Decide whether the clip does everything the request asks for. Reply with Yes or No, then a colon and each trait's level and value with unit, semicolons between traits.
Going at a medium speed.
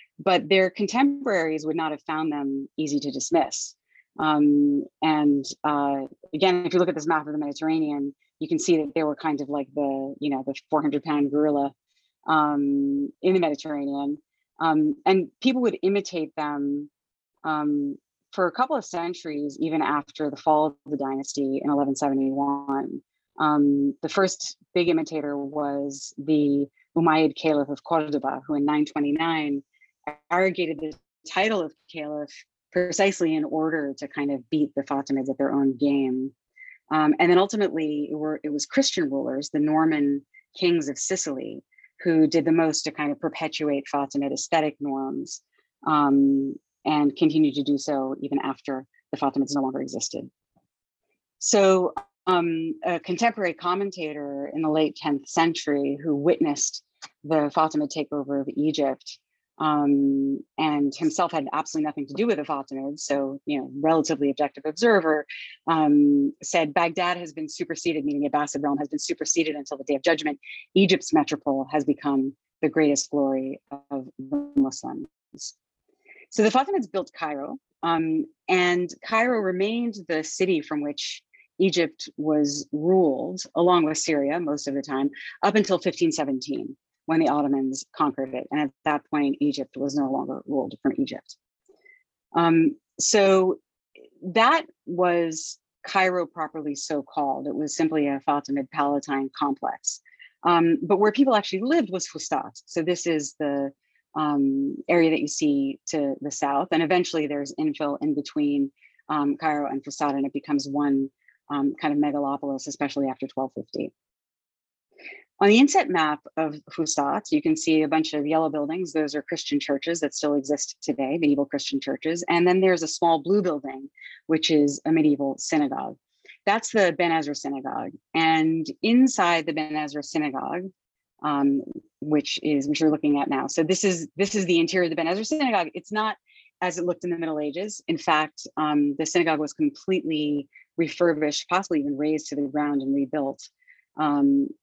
Yes: average, 160 wpm